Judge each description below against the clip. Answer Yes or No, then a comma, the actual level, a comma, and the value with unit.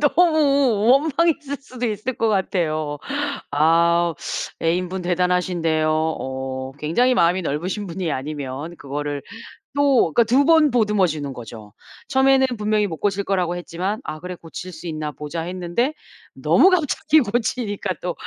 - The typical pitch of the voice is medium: Yes, medium, 180 Hz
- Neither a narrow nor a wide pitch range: No, wide, 7.2 semitones